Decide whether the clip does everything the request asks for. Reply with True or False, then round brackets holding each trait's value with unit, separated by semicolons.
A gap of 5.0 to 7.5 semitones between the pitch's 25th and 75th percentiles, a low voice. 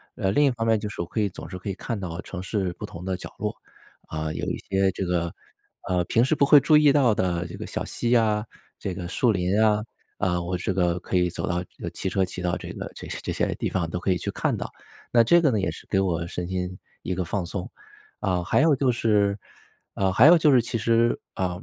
False (4.3 semitones; 95 Hz)